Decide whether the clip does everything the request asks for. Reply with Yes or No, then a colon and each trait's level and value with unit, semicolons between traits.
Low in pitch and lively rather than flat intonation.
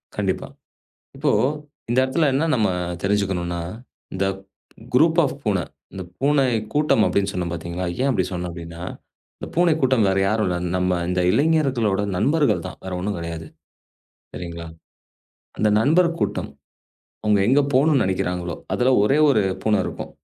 Yes: low, 105 Hz; wide, 7.0 semitones